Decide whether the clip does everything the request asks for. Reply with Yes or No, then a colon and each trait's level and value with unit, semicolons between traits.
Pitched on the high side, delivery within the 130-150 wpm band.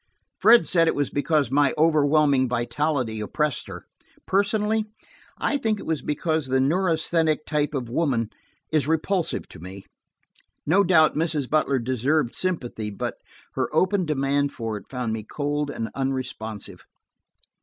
No: medium, 145 Hz; average, 145 wpm